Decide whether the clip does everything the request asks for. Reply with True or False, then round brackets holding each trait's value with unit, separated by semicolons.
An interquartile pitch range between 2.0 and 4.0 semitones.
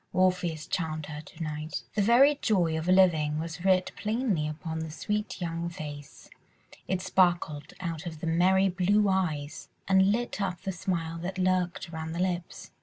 True (2.9 semitones)